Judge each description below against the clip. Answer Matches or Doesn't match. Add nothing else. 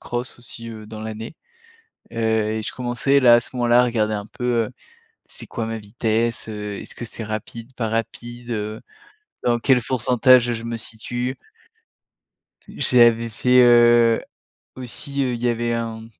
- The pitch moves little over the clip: Matches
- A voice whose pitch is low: Matches